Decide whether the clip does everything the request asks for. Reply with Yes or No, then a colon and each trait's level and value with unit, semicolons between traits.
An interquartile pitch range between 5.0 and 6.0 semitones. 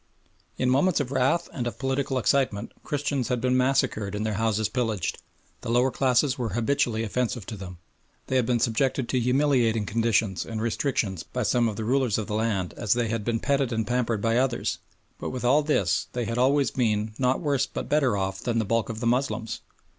No: average, 3.0 semitones